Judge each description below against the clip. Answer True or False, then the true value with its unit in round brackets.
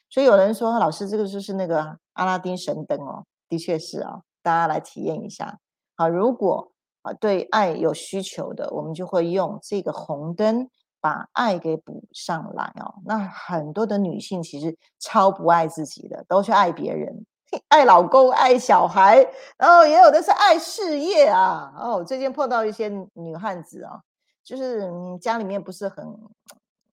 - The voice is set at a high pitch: True (200 Hz)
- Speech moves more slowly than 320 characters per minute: True (250 characters per minute)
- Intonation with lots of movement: True (6.1 semitones)